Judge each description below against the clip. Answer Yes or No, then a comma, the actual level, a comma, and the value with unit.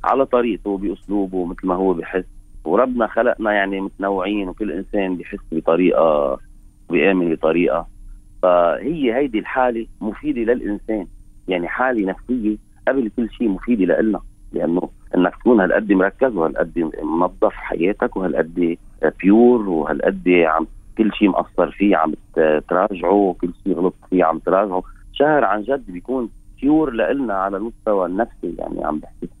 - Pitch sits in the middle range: No, low, 100 Hz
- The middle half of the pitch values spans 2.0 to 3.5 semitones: Yes, average, 2.9 semitones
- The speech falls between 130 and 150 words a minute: Yes, fast, 135 wpm